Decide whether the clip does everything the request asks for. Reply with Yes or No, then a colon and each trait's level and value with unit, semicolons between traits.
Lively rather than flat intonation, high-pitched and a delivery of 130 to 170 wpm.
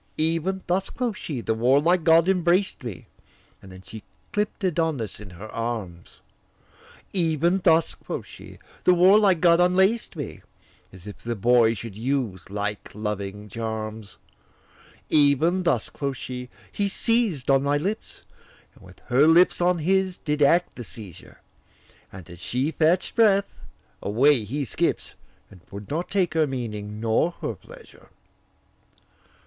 No: wide, 8.2 semitones; medium, 145 Hz; average, 145 wpm